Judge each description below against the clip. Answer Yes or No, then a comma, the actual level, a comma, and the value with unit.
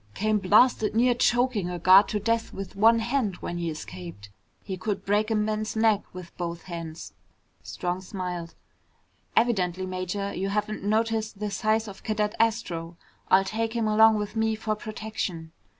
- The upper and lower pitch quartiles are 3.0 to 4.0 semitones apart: Yes, average, 3.3 semitones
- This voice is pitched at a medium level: No, high, 210 Hz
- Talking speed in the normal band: Yes, average, 165 wpm